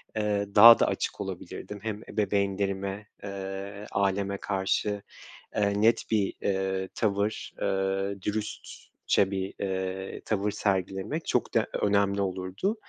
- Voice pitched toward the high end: No, low, 100 Hz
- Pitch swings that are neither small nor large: No, narrow, 1.2 semitones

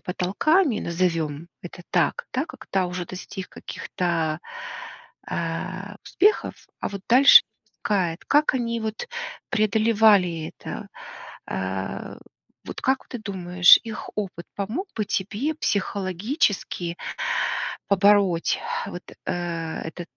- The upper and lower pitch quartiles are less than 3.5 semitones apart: No, average, 4.1 semitones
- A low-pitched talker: No, high, 190 Hz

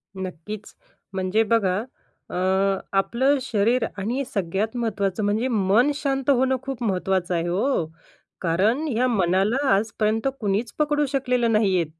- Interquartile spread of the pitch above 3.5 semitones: Yes, average, 4.7 semitones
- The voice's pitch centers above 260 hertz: No, high, 215 Hz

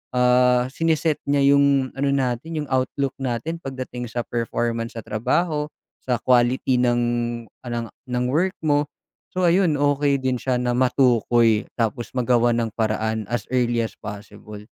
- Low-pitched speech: Yes, low, 125 Hz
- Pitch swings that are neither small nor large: Yes, average, 3.0 semitones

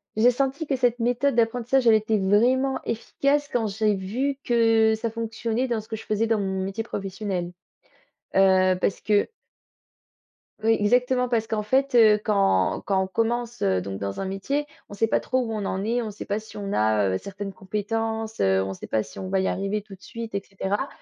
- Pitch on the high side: Yes, high, 220 Hz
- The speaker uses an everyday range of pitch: Yes, average, 3.4 semitones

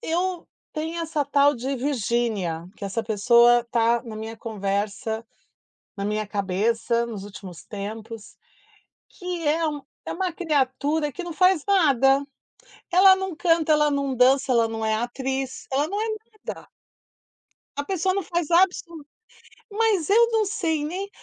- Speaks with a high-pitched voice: Yes, very high, 275 Hz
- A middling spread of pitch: No, wide, 7.0 semitones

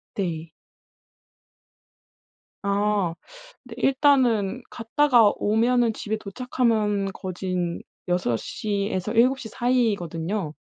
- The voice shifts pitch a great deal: No, average, 4.3 semitones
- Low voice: No, high, 210 Hz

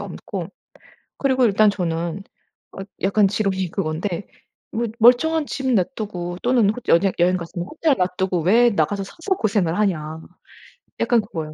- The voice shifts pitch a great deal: No, average, 4.7 semitones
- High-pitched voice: Yes, high, 195 Hz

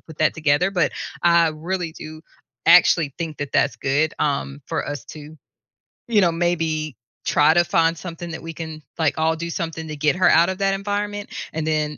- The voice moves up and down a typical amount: No, narrow, 2.0 semitones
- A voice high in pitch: No, medium, 160 Hz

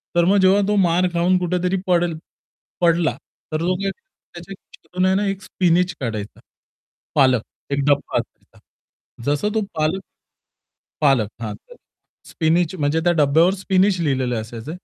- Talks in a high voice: No, medium, 170 Hz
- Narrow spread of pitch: No, average, 4.3 semitones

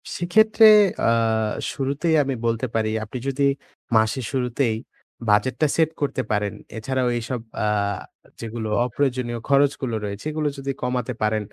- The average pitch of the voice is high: No, low, 125 Hz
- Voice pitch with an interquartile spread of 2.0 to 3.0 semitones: No, average, 3.8 semitones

